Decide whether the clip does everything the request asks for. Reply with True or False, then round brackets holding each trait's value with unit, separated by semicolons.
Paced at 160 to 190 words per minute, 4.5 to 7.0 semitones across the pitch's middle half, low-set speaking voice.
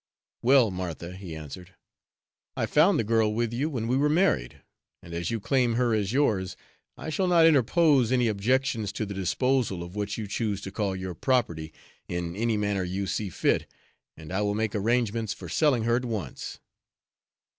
True (185 wpm; 4.9 semitones; 110 Hz)